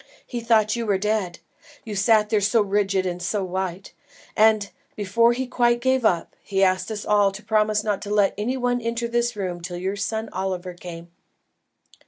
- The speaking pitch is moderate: No, high, 210 Hz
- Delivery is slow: No, average, 190 wpm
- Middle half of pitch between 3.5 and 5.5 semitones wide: No, average, 3.1 semitones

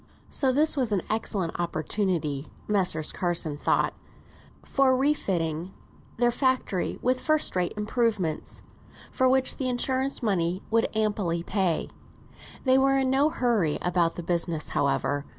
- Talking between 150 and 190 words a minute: No, slow, 135 wpm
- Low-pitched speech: No, high, 205 Hz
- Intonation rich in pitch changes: Yes, wide, 7.3 semitones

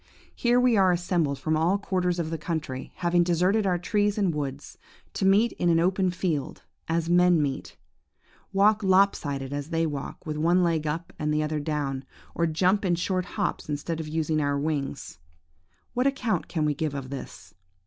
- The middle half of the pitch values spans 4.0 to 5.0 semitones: No, average, 3.6 semitones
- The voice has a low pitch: No, medium, 165 Hz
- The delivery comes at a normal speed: Yes, average, 190 wpm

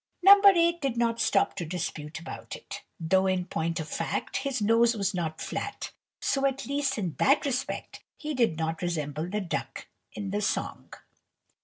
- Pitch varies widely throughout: Yes, wide, 8.3 semitones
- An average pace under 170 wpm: No, average, 175 wpm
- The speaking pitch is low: No, high, 205 Hz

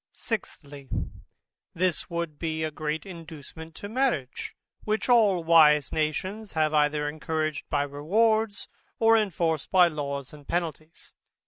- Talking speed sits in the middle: No, slow, 125 wpm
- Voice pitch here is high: No, medium, 160 Hz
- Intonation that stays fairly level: No, average, 4.0 semitones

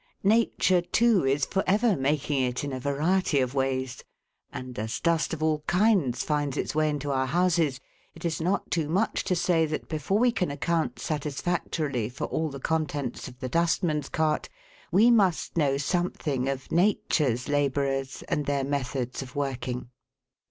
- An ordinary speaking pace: Yes, average, 165 wpm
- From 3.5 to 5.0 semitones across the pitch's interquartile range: Yes, average, 4.3 semitones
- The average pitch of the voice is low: No, medium, 150 Hz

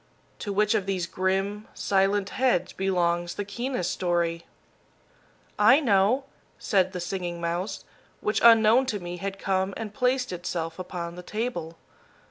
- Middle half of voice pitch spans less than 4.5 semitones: Yes, average, 3.3 semitones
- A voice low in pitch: No, high, 195 Hz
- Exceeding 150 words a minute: No, average, 140 wpm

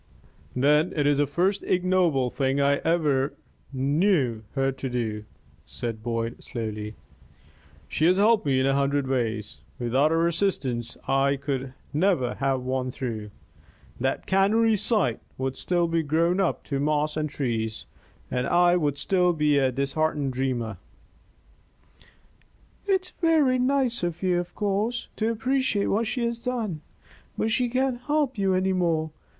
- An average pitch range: No, wide, 6.7 semitones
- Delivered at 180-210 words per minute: No, average, 150 wpm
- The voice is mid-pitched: Yes, medium, 150 Hz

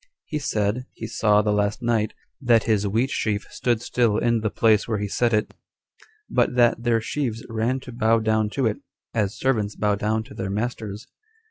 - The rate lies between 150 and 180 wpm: No, average, 195 wpm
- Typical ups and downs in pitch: No, narrow, 2.2 semitones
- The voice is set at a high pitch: No, low, 110 Hz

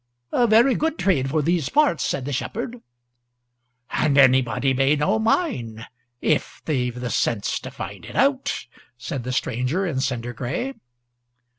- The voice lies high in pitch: No, medium, 140 Hz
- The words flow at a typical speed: Yes, average, 150 wpm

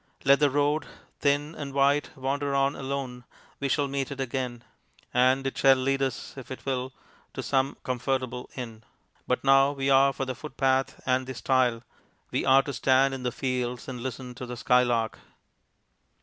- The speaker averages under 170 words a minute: No, average, 175 wpm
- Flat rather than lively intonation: Yes, narrow, 1.5 semitones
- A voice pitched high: No, low, 135 Hz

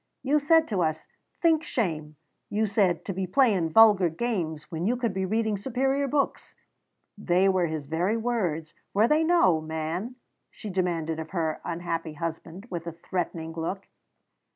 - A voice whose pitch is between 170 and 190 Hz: Yes, medium, 185 Hz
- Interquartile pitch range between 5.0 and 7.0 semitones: Yes, wide, 5.6 semitones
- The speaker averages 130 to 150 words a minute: No, average, 160 wpm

